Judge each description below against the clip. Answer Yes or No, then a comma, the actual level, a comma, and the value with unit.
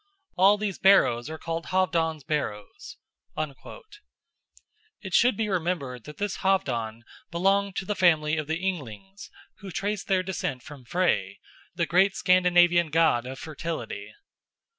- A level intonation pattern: No, average, 4.3 semitones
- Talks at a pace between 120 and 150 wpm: Yes, slow, 135 wpm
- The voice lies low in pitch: No, medium, 175 Hz